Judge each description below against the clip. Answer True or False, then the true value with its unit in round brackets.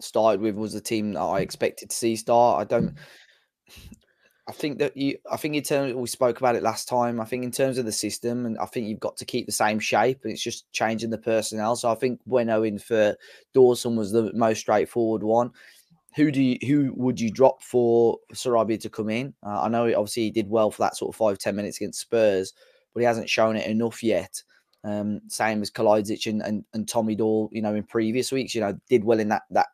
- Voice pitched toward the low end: True (115 Hz)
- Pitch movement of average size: False (2.3 semitones)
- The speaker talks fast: True (240 wpm)